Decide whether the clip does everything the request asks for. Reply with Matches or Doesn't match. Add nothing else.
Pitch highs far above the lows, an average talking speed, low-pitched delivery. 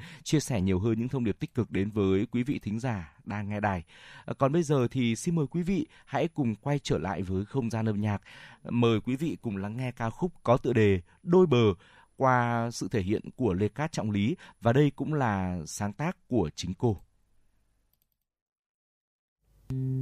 Doesn't match